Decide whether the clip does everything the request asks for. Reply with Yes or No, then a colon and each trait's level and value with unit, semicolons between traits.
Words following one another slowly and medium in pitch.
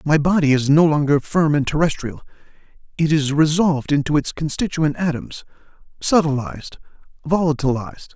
Yes: slow, 125 wpm; medium, 155 Hz